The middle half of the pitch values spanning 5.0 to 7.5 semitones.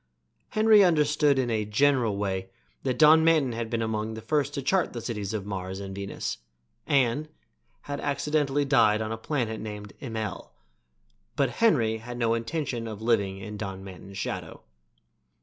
Yes: average, 5.3 semitones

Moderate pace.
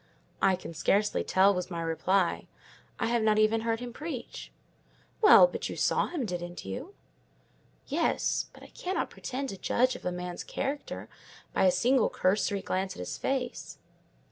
Yes: average, 170 wpm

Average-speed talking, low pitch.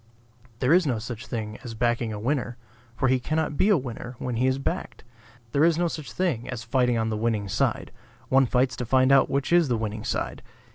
No: fast, 225 wpm; low, 125 Hz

